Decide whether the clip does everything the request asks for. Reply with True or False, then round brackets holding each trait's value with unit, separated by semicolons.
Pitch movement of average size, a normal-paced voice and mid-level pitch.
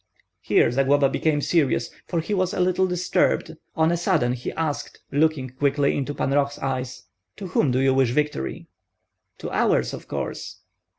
True (3.6 semitones; 170 wpm; 145 Hz)